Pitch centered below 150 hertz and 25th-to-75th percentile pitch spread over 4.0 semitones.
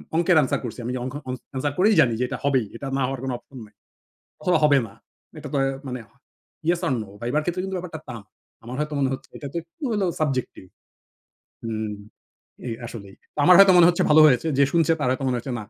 Yes: medium, 140 Hz; average, 5.1 semitones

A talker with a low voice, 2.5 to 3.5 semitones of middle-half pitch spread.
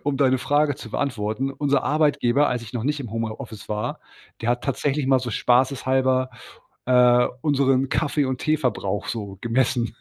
Yes: low, 130 Hz; average, 2.9 semitones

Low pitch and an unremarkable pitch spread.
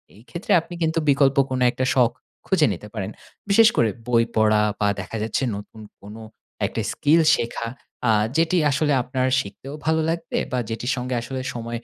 Yes: low, 125 Hz; average, 5.0 semitones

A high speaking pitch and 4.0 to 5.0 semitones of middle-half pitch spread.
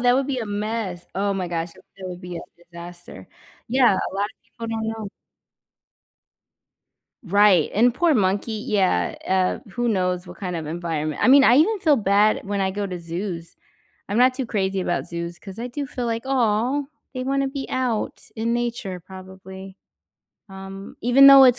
Yes: high, 205 Hz; average, 4.7 semitones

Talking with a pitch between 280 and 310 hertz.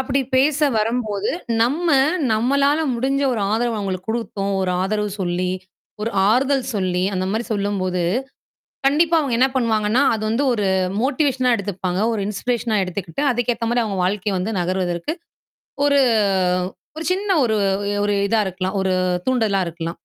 No: high, 220 Hz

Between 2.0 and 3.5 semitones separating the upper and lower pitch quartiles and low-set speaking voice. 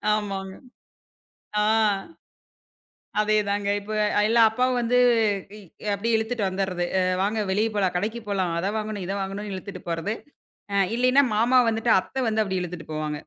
No: narrow, 2.6 semitones; high, 205 Hz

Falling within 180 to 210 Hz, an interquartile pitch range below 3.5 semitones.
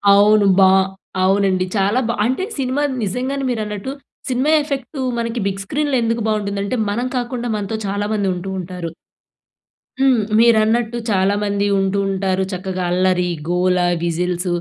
No: high, 205 Hz; average, 4.1 semitones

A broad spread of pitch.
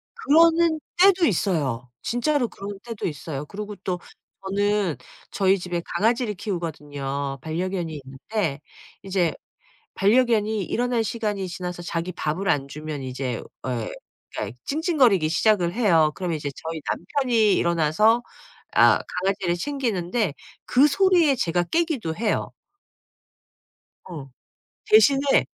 Yes: wide, 6.7 semitones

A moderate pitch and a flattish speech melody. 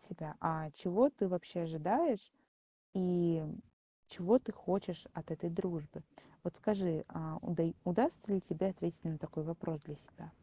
No: medium, 175 Hz; average, 3.2 semitones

